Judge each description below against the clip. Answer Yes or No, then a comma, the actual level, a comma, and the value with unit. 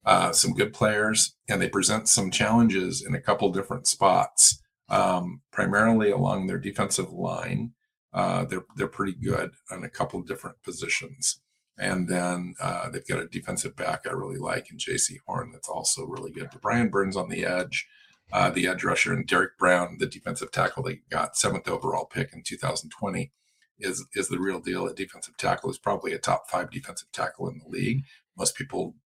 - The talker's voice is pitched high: No, low, 110 Hz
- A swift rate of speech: No, average, 185 wpm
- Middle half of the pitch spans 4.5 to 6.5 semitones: Yes, average, 5.0 semitones